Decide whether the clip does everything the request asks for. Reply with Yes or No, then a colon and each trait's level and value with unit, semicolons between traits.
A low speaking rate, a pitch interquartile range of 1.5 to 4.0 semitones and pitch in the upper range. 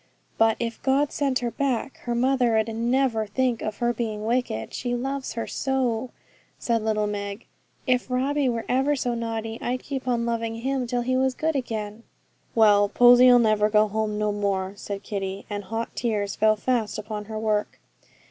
No: average, 180 wpm; average, 3.0 semitones; high, 230 Hz